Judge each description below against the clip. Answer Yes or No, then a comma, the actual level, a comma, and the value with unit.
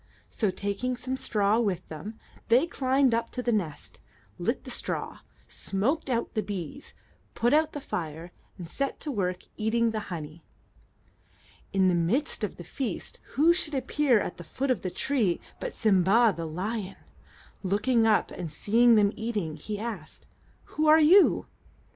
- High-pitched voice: Yes, high, 220 Hz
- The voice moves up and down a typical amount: No, wide, 5.7 semitones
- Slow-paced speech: No, average, 165 wpm